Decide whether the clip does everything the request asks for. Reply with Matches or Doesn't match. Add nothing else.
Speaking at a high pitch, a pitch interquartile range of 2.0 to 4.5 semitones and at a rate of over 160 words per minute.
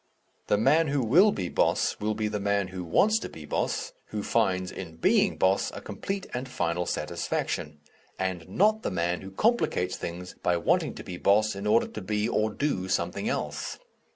Doesn't match